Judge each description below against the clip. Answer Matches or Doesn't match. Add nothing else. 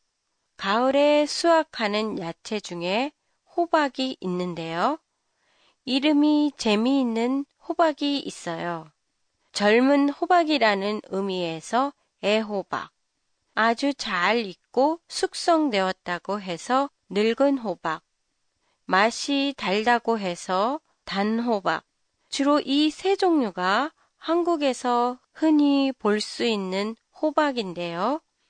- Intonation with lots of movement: Matches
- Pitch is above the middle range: Matches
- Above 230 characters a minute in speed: Doesn't match